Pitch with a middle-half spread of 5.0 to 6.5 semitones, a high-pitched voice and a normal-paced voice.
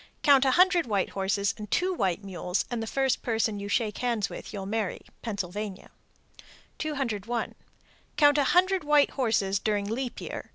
Yes: average, 5.3 semitones; high, 225 Hz; average, 165 wpm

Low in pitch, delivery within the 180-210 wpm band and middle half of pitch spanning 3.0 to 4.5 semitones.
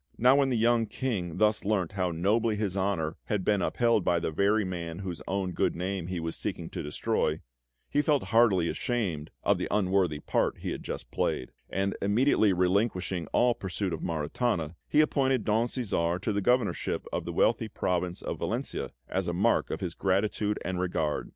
Yes: very low, 95 Hz; average, 190 wpm; average, 4.2 semitones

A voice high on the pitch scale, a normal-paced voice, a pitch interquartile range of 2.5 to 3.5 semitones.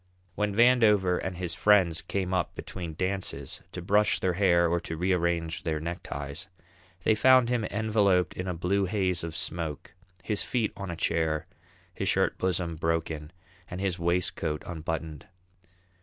No: very low, 90 Hz; average, 155 wpm; average, 3.2 semitones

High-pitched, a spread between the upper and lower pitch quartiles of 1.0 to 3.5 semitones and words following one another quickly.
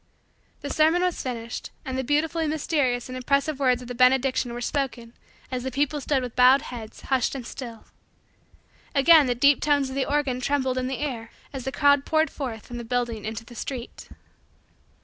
No: very high, 260 Hz; average, 2.7 semitones; average, 190 wpm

